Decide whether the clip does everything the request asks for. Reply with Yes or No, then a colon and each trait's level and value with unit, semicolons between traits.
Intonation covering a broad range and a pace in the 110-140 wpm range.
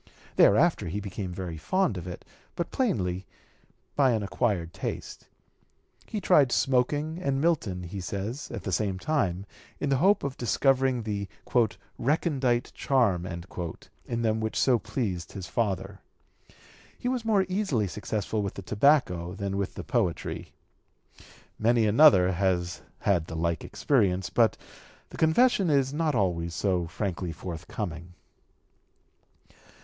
Yes: wide, 7.1 semitones; slow, 135 wpm